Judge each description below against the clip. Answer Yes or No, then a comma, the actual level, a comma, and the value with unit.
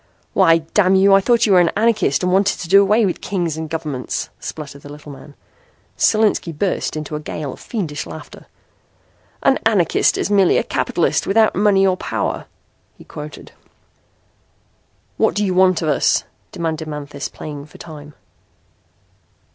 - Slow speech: No, average, 165 wpm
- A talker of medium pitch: Yes, medium, 170 Hz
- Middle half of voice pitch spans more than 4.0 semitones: Yes, average, 4.6 semitones